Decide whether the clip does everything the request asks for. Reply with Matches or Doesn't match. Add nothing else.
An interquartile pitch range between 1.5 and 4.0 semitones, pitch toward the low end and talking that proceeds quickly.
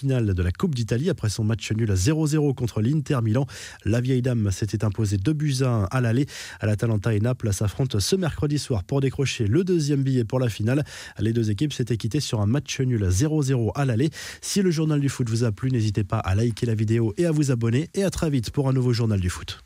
Doesn't match